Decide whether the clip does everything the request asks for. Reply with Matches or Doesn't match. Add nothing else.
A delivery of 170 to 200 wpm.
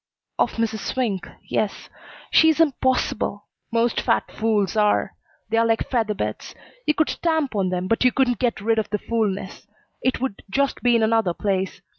Matches